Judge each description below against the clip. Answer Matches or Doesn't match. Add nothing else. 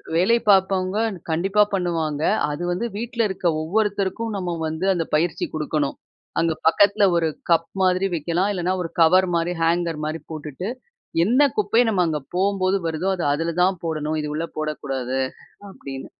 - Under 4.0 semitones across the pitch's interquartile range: Matches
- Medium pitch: Matches